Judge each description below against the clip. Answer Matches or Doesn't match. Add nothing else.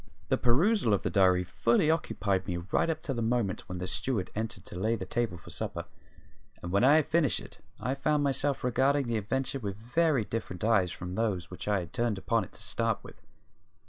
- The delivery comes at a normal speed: Doesn't match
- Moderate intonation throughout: Doesn't match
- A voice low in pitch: Matches